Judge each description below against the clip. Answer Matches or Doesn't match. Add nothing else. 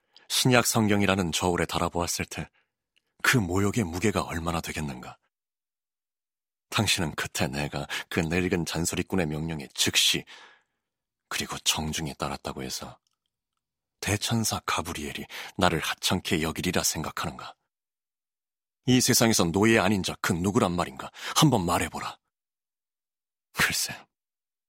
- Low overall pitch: Matches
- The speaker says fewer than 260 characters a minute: Doesn't match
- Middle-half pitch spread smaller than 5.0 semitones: Matches